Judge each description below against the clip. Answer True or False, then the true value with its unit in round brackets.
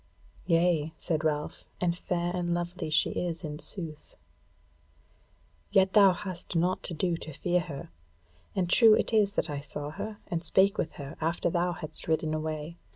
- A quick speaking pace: False (170 wpm)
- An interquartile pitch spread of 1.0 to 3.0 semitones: True (2.5 semitones)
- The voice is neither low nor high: True (170 Hz)